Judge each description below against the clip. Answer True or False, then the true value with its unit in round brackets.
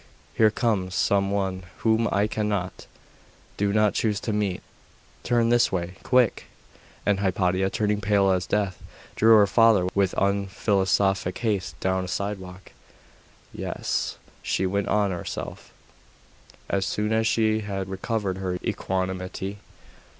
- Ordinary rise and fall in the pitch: False (2.1 semitones)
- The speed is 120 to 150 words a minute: True (135 wpm)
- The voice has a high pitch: False (100 Hz)